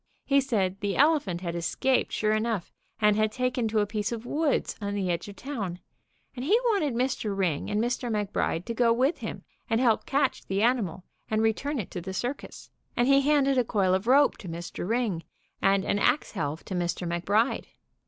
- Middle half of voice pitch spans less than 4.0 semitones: No, average, 4.9 semitones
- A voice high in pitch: Yes, high, 220 Hz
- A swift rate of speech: Yes, fast, 215 wpm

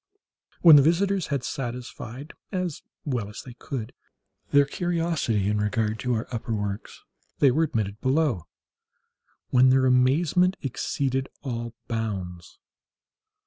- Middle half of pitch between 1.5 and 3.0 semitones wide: No, average, 4.9 semitones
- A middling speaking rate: No, slow, 125 wpm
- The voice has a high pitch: No, low, 130 Hz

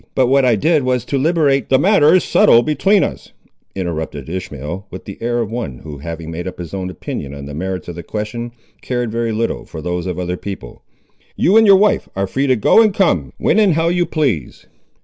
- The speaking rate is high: Yes, fast, 225 wpm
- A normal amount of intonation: No, wide, 8.5 semitones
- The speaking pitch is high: No, low, 110 Hz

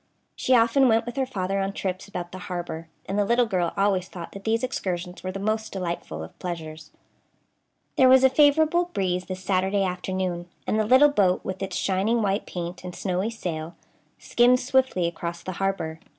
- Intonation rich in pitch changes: No, average, 4.2 semitones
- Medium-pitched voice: No, high, 195 Hz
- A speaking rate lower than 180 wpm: No, average, 190 wpm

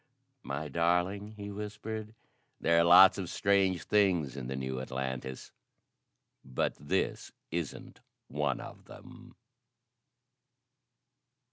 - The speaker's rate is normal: No, slow, 105 wpm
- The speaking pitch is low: Yes, very low, 85 Hz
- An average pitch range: No, wide, 6.9 semitones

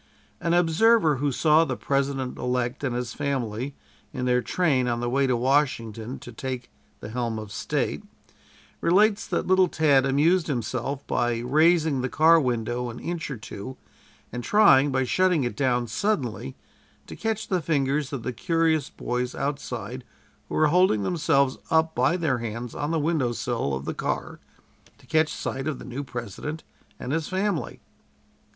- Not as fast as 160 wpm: No, average, 170 wpm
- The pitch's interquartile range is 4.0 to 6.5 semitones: Yes, average, 4.6 semitones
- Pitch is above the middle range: No, low, 135 Hz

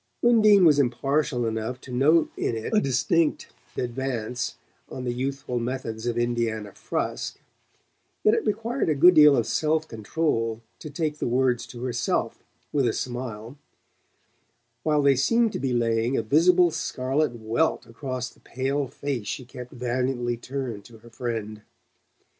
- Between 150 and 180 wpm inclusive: Yes, average, 155 wpm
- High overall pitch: No, low, 125 Hz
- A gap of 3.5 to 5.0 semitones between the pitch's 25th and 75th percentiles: Yes, average, 3.9 semitones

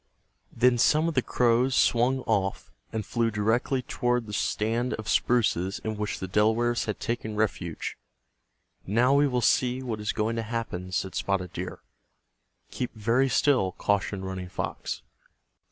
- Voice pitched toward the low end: Yes, low, 115 Hz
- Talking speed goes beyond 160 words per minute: No, average, 155 wpm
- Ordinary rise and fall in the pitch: Yes, average, 3.1 semitones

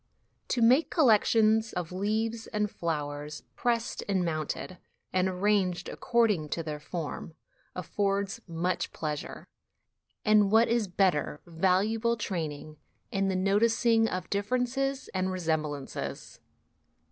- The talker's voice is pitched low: No, high, 195 Hz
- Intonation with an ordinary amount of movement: Yes, average, 4.9 semitones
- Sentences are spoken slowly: Yes, slow, 125 wpm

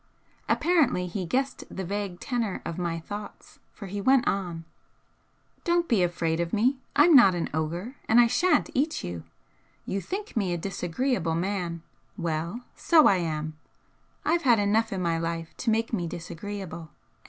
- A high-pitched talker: Yes, high, 195 Hz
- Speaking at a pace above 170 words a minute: No, average, 165 wpm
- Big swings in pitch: Yes, wide, 6.3 semitones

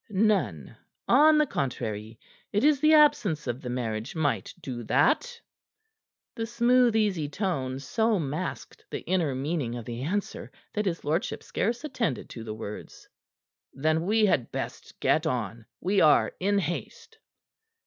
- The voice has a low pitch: No, medium, 165 Hz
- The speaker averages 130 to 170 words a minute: Yes, average, 150 wpm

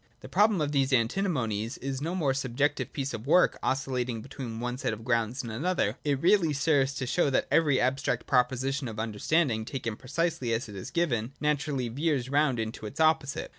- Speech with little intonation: No, average, 4.1 semitones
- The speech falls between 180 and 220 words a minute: Yes, average, 190 wpm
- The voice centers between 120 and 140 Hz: Yes, low, 135 Hz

